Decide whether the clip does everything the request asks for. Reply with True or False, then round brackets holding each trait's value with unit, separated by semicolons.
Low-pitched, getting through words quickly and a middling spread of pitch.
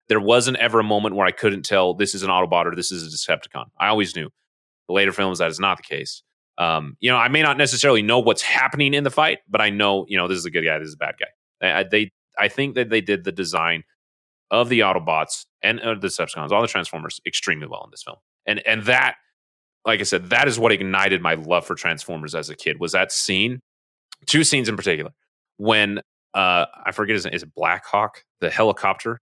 True (105 Hz; 240 wpm; 4.4 semitones)